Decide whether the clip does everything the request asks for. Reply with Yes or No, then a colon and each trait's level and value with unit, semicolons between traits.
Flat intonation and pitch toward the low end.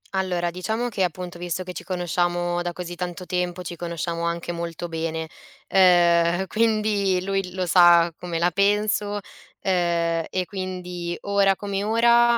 No: narrow, 2.0 semitones; medium, 180 Hz